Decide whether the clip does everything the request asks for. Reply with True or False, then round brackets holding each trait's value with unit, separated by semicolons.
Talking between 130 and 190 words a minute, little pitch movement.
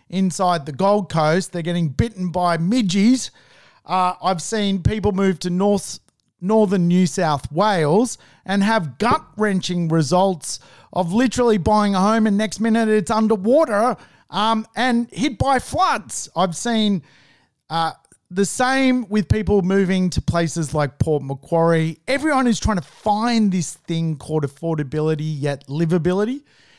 False (145 wpm; 4.9 semitones)